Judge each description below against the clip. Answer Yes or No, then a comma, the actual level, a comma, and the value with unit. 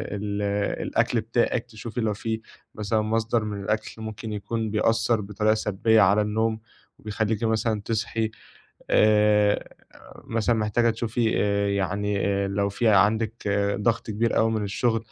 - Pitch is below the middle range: Yes, low, 110 Hz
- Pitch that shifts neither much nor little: No, narrow, 1.5 semitones